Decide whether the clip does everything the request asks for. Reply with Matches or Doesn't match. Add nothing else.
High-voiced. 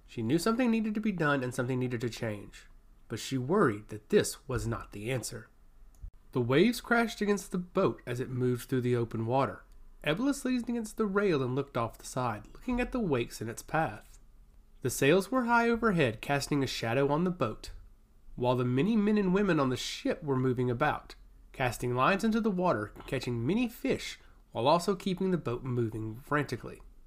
Doesn't match